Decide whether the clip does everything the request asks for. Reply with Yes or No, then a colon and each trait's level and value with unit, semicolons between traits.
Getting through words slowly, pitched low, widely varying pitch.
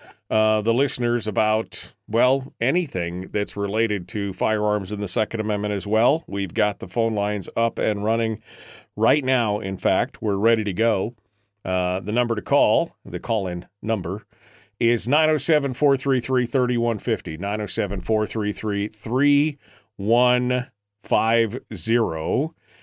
No: slow, 115 wpm; low, 110 Hz; average, 2.7 semitones